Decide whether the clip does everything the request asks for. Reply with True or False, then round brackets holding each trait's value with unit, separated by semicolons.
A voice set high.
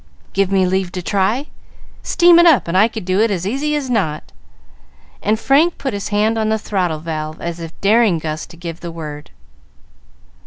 True (195 Hz)